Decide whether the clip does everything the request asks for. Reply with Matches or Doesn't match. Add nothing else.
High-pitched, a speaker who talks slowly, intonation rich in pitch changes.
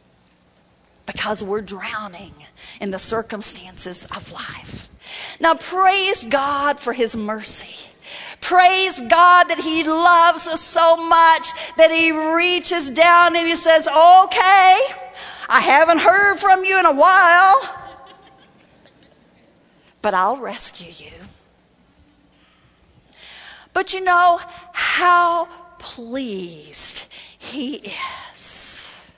Matches